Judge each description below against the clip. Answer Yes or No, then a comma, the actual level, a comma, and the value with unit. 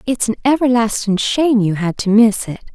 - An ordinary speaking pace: Yes, average, 195 wpm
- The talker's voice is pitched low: No, high, 225 Hz